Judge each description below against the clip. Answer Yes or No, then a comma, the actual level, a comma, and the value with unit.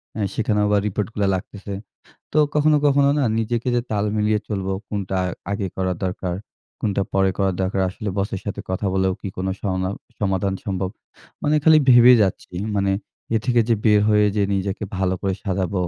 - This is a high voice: No, low, 100 Hz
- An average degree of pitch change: No, narrow, 2.2 semitones